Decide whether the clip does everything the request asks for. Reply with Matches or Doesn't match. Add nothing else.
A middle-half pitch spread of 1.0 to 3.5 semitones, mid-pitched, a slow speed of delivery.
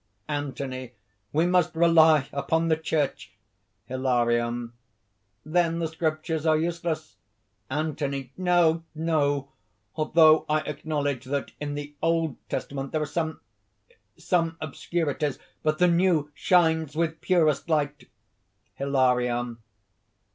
Matches